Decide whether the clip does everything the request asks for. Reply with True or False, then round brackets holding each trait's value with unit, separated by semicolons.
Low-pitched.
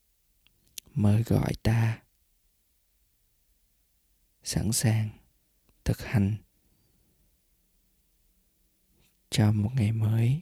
True (105 Hz)